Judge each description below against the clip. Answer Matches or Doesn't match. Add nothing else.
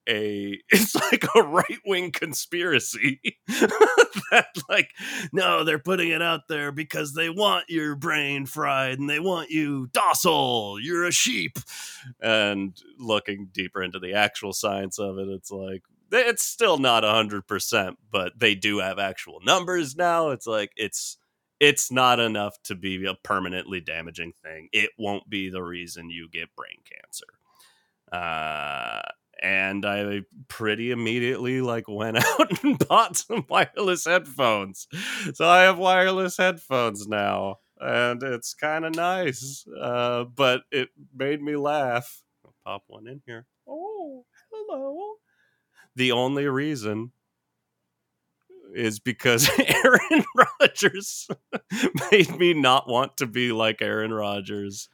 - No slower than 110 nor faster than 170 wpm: Matches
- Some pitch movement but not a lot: Doesn't match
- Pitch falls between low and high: Doesn't match